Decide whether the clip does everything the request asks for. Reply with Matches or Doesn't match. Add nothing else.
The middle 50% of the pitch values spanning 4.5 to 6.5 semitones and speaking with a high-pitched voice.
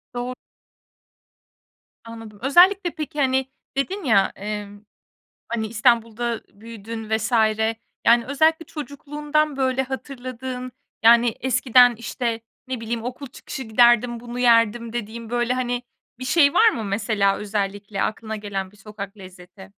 Doesn't match